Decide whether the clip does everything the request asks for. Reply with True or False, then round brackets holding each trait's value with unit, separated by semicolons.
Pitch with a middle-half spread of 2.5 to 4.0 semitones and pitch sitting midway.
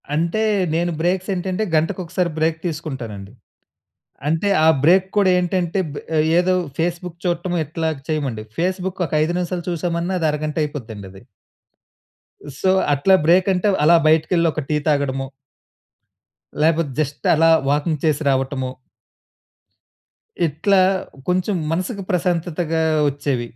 True (3.2 semitones; 165 Hz)